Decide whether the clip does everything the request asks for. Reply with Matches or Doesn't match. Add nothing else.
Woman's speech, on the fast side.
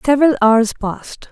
Doesn't match